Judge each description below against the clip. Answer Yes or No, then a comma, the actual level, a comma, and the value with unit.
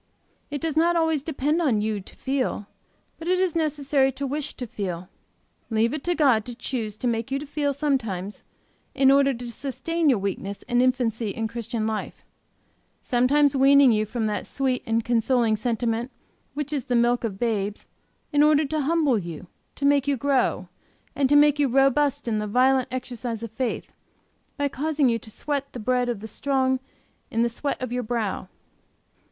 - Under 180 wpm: No, average, 185 wpm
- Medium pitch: No, very high, 255 Hz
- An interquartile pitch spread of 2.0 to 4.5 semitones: Yes, average, 3.9 semitones